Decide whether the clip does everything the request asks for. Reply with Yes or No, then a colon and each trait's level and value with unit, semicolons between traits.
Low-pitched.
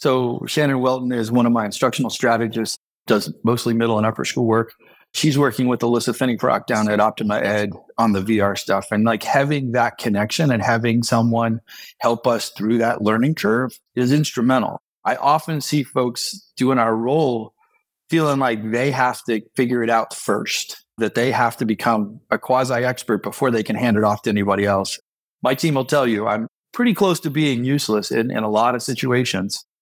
Yes: low, 120 Hz